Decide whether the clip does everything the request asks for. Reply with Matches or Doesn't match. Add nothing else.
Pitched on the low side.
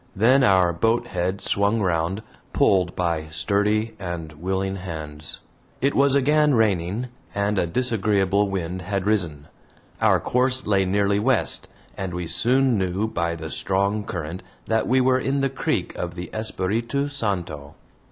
Matches